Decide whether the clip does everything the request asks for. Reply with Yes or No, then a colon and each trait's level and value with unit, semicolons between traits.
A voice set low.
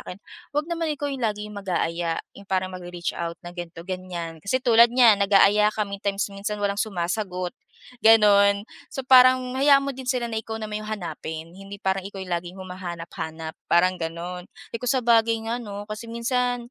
No: high, 200 Hz